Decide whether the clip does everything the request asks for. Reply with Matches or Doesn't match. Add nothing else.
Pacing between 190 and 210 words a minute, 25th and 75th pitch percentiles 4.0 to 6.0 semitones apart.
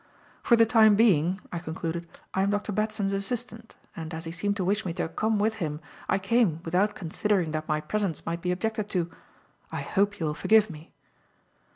Matches